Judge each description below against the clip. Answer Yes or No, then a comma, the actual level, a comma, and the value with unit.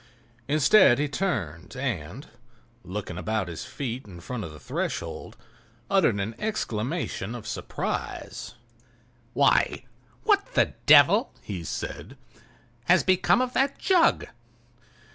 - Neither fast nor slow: No, slow, 110 wpm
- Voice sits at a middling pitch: No, low, 120 Hz